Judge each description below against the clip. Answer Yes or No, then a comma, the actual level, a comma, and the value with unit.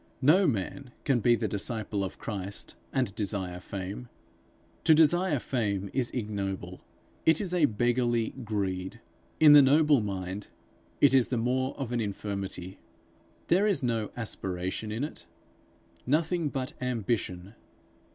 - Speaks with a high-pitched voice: No, low, 115 Hz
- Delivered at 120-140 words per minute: Yes, slow, 135 wpm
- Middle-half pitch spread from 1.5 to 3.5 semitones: No, wide, 5.5 semitones